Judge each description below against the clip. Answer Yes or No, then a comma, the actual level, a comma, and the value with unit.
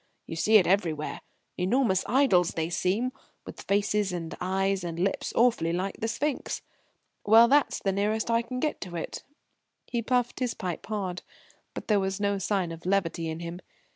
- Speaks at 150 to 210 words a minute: Yes, average, 175 wpm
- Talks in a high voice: Yes, high, 195 Hz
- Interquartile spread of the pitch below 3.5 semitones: No, average, 4.3 semitones